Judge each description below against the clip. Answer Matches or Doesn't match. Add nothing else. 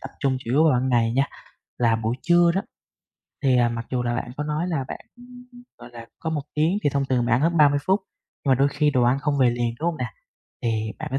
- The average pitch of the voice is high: Doesn't match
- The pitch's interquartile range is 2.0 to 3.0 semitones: Doesn't match